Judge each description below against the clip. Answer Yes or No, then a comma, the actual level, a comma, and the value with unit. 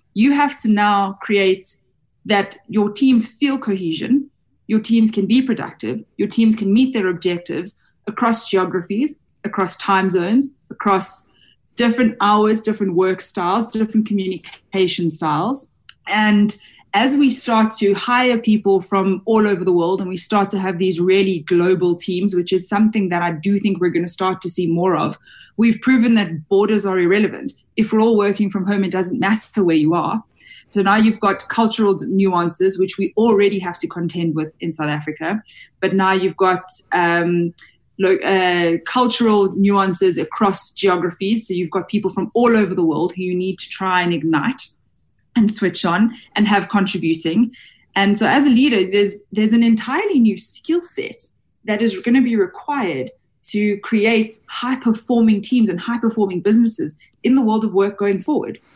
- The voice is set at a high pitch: Yes, high, 200 Hz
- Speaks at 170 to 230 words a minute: Yes, average, 175 wpm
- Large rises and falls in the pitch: No, average, 3.1 semitones